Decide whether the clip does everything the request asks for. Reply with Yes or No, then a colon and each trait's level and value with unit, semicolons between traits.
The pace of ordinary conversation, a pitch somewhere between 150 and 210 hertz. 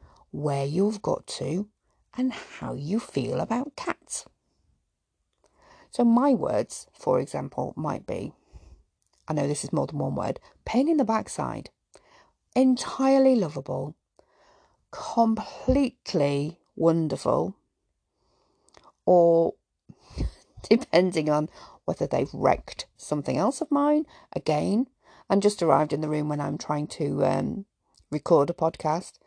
No: slow, 120 wpm; medium, 185 Hz